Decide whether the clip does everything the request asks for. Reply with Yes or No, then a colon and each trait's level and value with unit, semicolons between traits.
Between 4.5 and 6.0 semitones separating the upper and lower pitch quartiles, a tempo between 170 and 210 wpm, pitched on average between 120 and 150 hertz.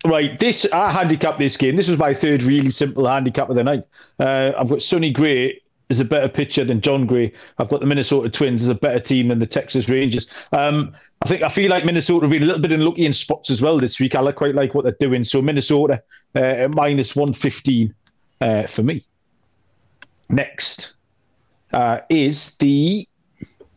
No: average, 2.9 semitones; average, 200 wpm; medium, 140 Hz